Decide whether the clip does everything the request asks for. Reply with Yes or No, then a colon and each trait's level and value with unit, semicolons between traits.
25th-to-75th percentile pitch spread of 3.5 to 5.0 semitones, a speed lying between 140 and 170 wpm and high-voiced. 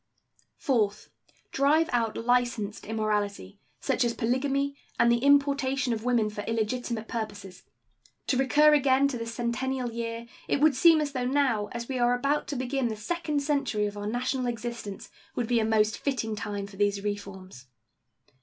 Yes: average, 4.0 semitones; average, 165 wpm; high, 240 Hz